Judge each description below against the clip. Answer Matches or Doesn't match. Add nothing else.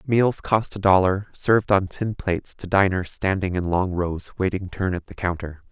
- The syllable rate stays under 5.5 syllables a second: Matches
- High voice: Doesn't match